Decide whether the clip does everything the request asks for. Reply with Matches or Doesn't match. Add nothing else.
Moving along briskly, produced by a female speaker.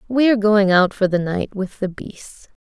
Matches